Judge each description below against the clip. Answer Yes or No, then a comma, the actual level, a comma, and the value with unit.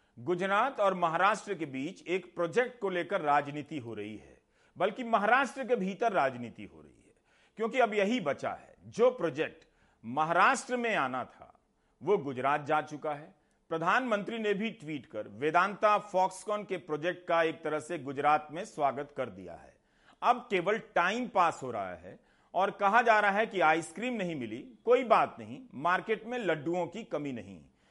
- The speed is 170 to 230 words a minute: Yes, average, 175 wpm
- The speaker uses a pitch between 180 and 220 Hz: Yes, medium, 185 Hz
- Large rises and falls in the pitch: Yes, wide, 6.3 semitones